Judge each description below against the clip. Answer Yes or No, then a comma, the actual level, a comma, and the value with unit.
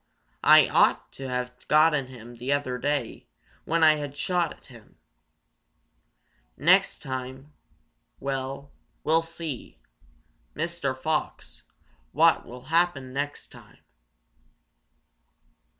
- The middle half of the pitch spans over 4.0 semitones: No, average, 3.6 semitones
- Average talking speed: No, slow, 105 wpm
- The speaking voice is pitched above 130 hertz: Yes, medium, 140 Hz